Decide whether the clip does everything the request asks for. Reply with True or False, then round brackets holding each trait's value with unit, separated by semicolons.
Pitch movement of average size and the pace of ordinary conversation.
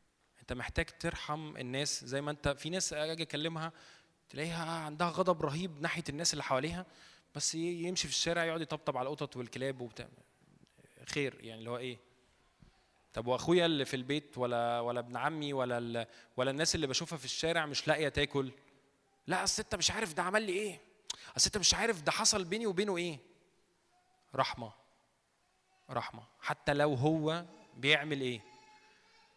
False (4.5 semitones; 155 wpm)